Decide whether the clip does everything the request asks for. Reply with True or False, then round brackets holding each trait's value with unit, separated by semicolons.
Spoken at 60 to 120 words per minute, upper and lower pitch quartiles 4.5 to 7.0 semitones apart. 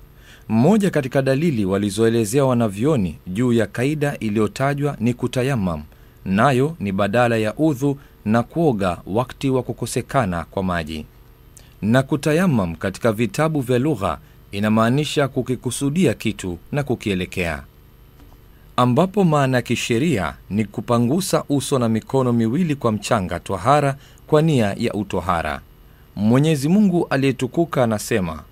True (115 wpm; 5.2 semitones)